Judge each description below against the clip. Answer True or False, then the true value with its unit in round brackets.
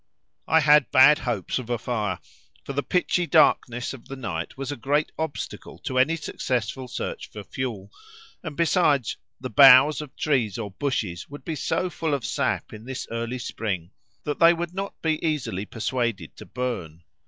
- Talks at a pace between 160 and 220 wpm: True (175 wpm)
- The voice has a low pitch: True (130 Hz)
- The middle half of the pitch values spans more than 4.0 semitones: True (4.8 semitones)